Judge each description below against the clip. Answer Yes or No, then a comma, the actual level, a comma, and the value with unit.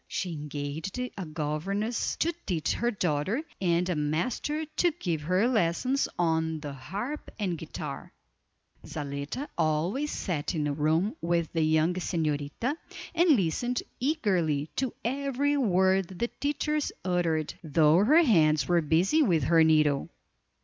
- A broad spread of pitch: Yes, wide, 7.6 semitones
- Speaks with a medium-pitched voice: Yes, medium, 175 Hz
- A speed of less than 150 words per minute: Yes, slow, 135 wpm